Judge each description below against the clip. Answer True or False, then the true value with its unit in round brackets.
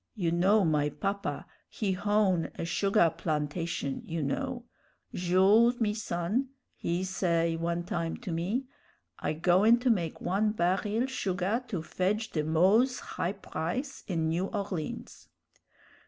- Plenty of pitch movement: False (4.2 semitones)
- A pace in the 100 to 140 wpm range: True (135 wpm)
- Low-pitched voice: False (185 Hz)